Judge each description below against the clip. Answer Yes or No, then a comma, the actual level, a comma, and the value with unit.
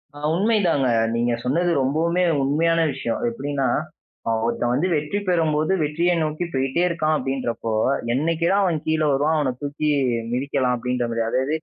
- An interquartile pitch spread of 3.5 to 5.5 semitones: Yes, average, 4.1 semitones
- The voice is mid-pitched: Yes, medium, 150 Hz